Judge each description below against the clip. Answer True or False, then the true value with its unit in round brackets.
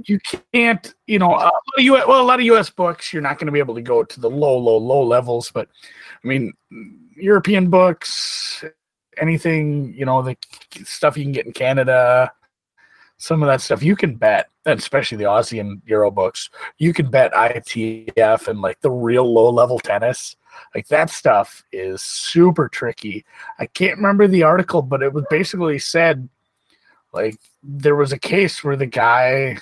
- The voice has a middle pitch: True (150 Hz)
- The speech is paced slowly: False (180 wpm)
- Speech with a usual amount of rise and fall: False (6.7 semitones)